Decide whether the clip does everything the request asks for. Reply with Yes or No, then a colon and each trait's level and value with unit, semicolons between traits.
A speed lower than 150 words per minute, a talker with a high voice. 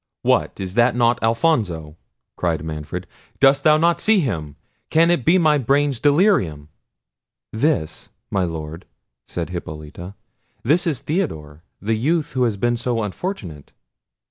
No: average, 140 wpm; low, 115 Hz